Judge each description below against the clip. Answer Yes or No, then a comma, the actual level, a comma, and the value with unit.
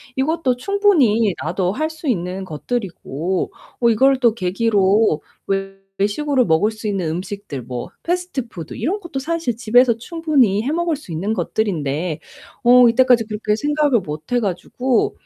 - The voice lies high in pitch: Yes, high, 225 Hz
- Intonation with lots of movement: Yes, wide, 5.9 semitones